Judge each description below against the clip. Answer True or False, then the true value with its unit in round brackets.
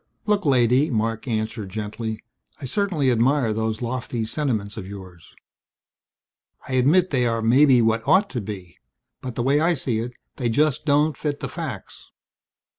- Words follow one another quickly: False (160 wpm)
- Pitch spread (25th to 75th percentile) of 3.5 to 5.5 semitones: True (4.6 semitones)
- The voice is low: True (120 Hz)